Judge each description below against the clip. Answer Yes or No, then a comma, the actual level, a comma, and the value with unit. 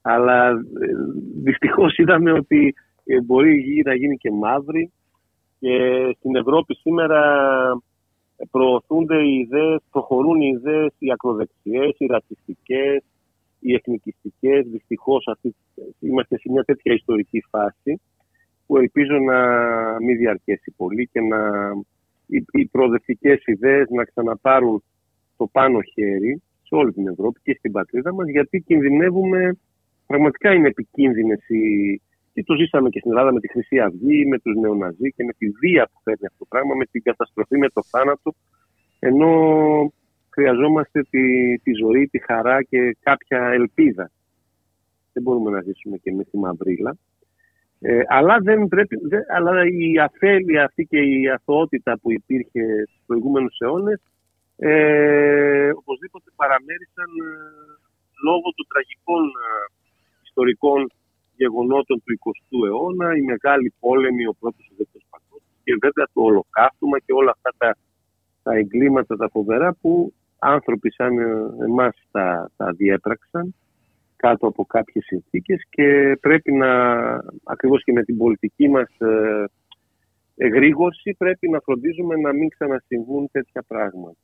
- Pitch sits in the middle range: No, low, 130 Hz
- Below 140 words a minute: Yes, average, 130 wpm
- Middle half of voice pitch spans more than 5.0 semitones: Yes, wide, 5.4 semitones